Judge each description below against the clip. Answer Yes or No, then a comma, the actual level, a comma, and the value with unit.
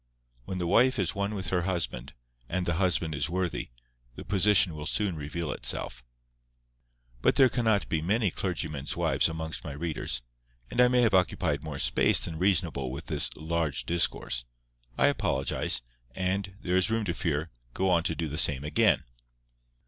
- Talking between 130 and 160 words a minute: No, average, 170 wpm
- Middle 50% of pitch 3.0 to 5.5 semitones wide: Yes, average, 3.7 semitones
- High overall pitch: No, very low, 85 Hz